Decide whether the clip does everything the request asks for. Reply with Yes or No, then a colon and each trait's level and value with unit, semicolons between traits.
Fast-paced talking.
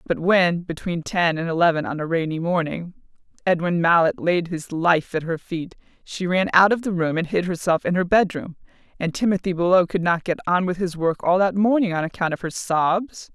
Yes: fast, 215 wpm